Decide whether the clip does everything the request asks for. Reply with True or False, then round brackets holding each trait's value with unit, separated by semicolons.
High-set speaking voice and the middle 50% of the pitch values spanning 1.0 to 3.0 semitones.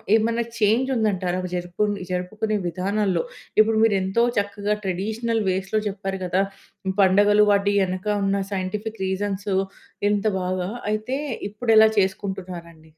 True (200 Hz; 2.5 semitones)